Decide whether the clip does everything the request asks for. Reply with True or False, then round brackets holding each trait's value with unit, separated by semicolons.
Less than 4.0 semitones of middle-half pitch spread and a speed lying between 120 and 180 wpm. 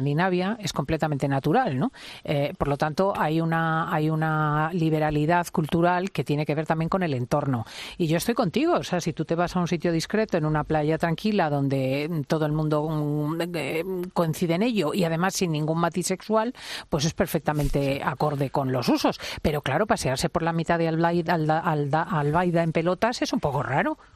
False (2.8 semitones; 190 wpm)